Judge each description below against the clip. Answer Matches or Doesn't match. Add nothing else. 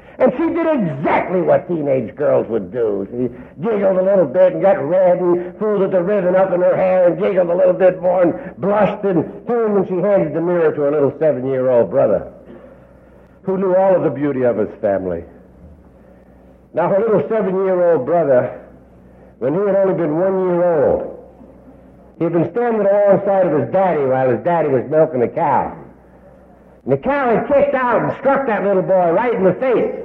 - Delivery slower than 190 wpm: Doesn't match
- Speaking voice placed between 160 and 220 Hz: Matches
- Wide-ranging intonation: Matches